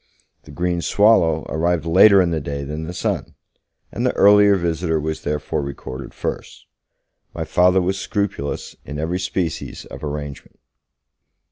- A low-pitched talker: Yes, very low, 85 Hz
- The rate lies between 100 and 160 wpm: Yes, average, 145 wpm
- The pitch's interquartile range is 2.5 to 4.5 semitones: Yes, average, 3.6 semitones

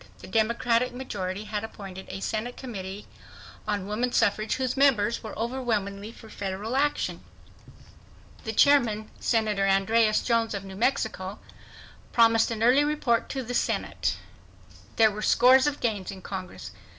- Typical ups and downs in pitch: Yes, average, 3.3 semitones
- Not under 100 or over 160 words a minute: Yes, average, 140 wpm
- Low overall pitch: No, high, 220 Hz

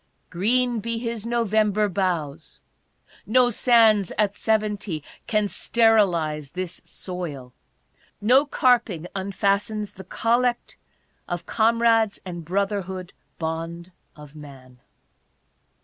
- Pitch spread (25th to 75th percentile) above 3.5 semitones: Yes, average, 4.9 semitones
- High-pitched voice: Yes, high, 200 Hz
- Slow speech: Yes, slow, 100 wpm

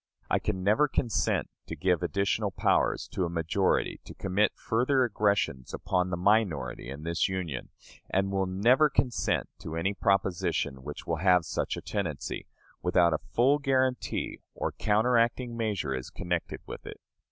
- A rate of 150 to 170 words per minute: Yes, average, 155 wpm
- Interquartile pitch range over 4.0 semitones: Yes, average, 4.6 semitones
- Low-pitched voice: Yes, very low, 95 Hz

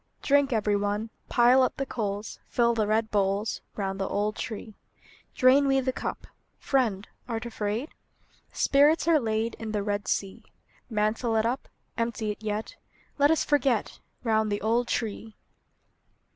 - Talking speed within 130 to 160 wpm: Yes, average, 155 wpm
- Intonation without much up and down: No, average, 3.3 semitones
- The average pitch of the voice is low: No, high, 225 Hz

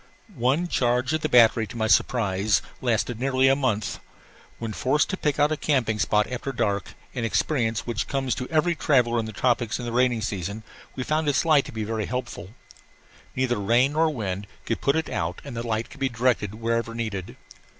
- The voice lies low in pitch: Yes, low, 120 Hz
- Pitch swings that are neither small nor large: Yes, average, 3.5 semitones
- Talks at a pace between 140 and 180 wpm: No, average, 190 wpm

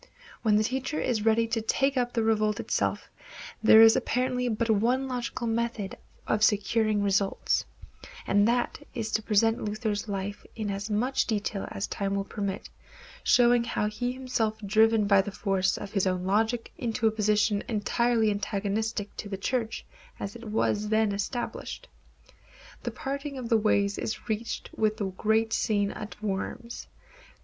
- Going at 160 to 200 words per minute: Yes, average, 165 wpm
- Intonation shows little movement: Yes, narrow, 2.3 semitones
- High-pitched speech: Yes, high, 220 Hz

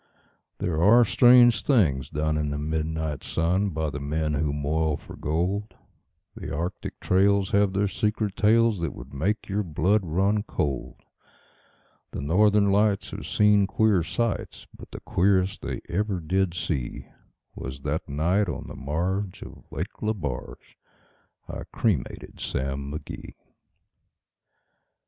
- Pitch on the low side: Yes, very low, 90 Hz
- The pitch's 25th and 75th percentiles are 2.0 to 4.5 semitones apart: No, average, 5.1 semitones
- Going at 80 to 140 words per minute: Yes, slow, 135 wpm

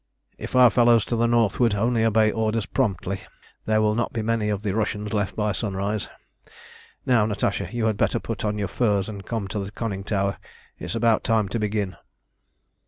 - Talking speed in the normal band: Yes, average, 190 wpm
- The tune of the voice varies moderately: No, narrow, 2.1 semitones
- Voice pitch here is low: Yes, low, 110 Hz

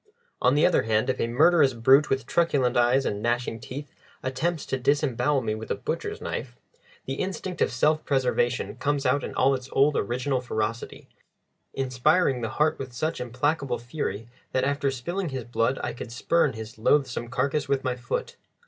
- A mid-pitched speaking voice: No, low, 130 Hz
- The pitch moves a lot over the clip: No, average, 3.2 semitones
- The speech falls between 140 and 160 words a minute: No, average, 180 wpm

